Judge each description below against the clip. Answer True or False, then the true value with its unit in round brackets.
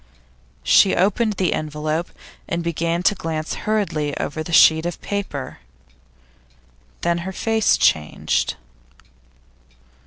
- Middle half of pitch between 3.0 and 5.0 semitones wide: True (3.7 semitones)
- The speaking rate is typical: False (105 wpm)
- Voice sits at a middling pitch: True (170 Hz)